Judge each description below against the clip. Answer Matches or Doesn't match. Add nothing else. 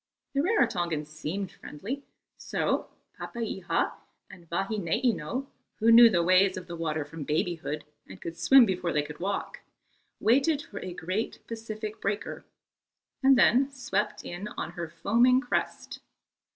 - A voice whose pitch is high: Matches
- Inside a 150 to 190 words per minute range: Doesn't match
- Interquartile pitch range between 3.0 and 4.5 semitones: Doesn't match